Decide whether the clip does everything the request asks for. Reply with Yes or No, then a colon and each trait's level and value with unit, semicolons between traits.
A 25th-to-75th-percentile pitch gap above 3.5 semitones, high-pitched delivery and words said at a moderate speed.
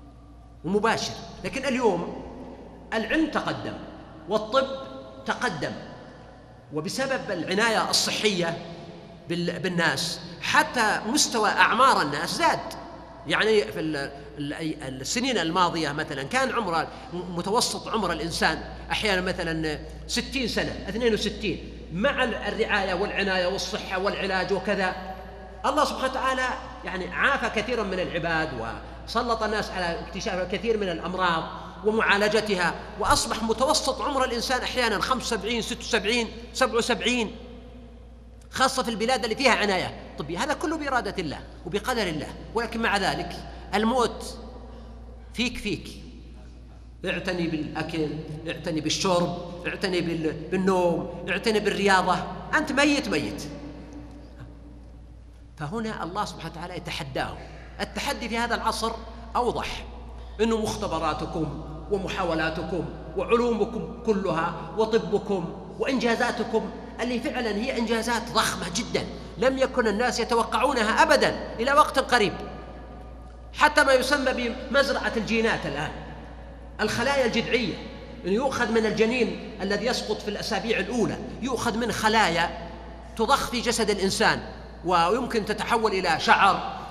Yes: wide, 5.6 semitones; high, 210 Hz; average, 105 wpm